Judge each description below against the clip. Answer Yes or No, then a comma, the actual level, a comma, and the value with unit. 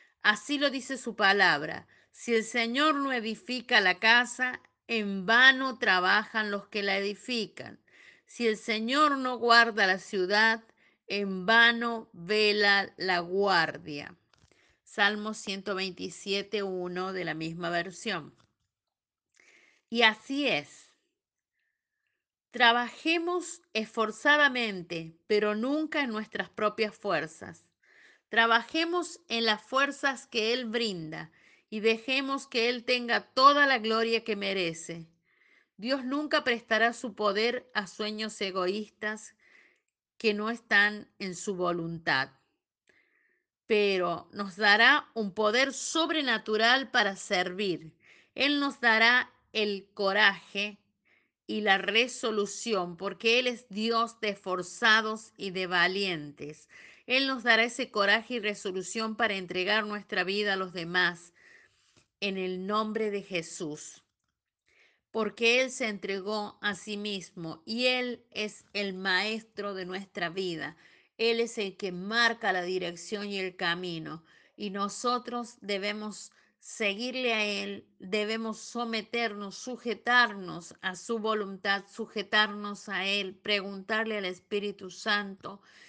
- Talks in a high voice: Yes, high, 215 Hz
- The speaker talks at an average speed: No, slow, 115 wpm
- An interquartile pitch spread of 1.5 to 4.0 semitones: Yes, average, 3.4 semitones